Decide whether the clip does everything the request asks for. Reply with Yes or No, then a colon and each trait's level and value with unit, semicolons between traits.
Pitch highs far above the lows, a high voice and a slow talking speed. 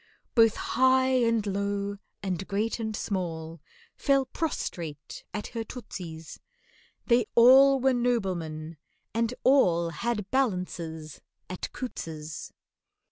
Yes: wide, 6.4 semitones; high, 205 Hz; slow, 105 wpm